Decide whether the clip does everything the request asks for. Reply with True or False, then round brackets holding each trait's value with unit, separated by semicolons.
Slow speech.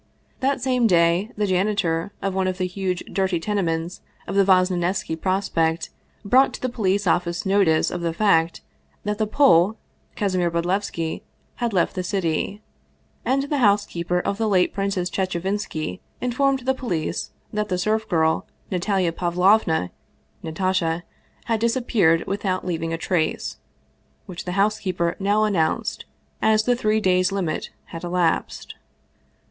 False (145 wpm)